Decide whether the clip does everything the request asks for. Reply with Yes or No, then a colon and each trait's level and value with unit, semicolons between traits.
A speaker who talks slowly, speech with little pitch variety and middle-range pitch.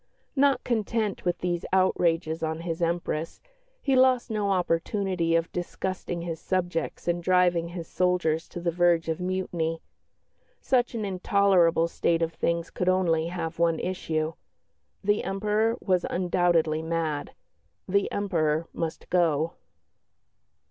Yes: slow, 130 wpm; narrow, 2.3 semitones; medium, 175 Hz